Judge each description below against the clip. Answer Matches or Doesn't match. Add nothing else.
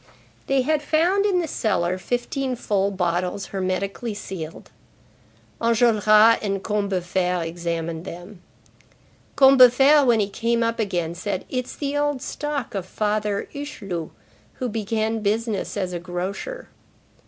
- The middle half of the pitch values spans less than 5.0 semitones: Doesn't match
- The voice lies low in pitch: Doesn't match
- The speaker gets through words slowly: Matches